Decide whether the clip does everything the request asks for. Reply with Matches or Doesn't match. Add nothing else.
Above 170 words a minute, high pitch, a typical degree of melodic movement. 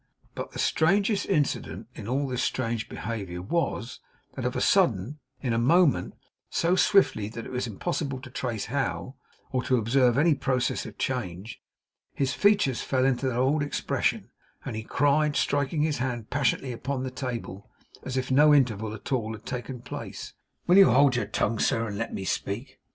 Doesn't match